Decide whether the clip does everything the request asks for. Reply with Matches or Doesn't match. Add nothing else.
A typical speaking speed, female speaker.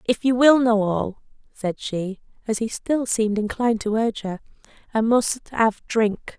Matches